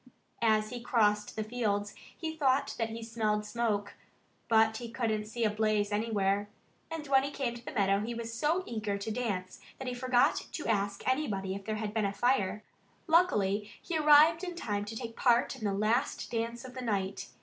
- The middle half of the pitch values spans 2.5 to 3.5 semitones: Yes, average, 3.2 semitones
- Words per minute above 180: Yes, average, 200 wpm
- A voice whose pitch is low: No, high, 225 Hz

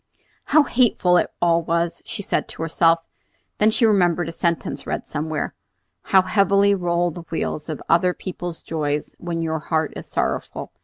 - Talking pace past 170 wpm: No, average, 165 wpm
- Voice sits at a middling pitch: Yes, medium, 170 Hz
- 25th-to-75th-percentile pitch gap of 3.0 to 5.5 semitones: No, narrow, 2.4 semitones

